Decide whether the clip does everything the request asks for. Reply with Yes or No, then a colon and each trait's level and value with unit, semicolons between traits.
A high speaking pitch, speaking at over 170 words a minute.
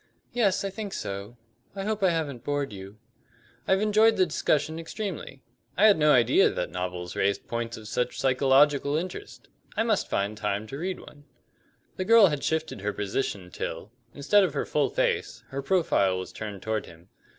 No: medium, 140 Hz; average, 180 wpm